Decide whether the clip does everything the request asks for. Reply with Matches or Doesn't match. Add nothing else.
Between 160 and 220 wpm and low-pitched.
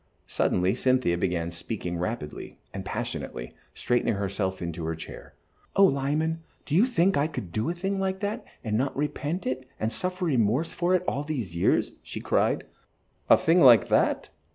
Matches